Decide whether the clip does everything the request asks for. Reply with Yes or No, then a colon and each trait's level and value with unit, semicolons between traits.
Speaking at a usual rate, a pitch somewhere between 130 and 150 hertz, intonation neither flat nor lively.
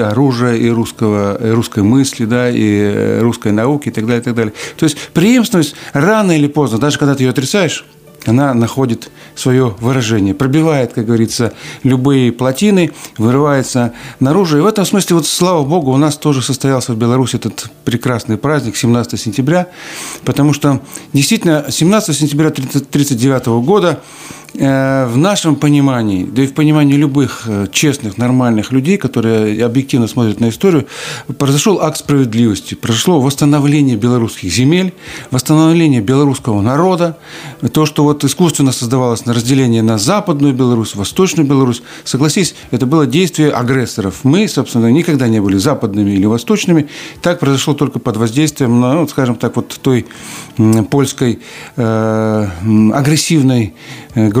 Yes: average, 140 wpm; low, 135 Hz; average, 4.5 semitones